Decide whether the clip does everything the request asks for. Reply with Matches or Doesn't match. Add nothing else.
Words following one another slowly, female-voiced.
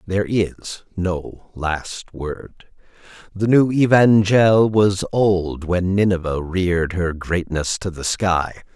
Doesn't match